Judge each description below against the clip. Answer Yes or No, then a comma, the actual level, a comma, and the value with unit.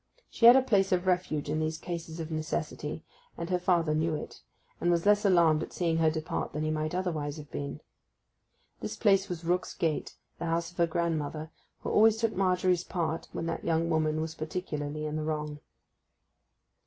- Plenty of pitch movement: No, narrow, 2.5 semitones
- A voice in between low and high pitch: Yes, medium, 165 Hz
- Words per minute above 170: Yes, average, 190 wpm